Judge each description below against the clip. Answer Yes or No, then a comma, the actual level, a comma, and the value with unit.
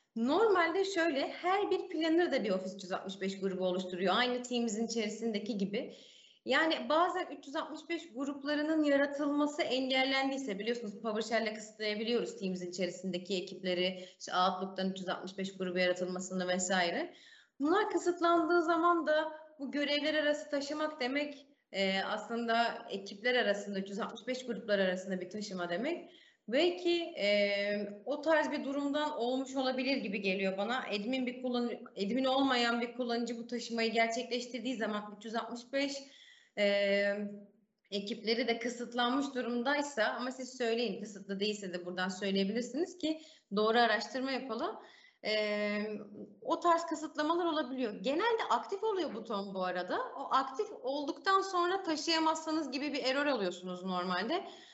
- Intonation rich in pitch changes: Yes, wide, 6.7 semitones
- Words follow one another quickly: No, average, 120 wpm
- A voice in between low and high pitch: No, high, 245 Hz